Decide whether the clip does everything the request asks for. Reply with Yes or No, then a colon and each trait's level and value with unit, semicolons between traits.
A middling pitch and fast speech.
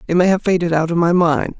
Yes: medium, 170 Hz; fast, 300 wpm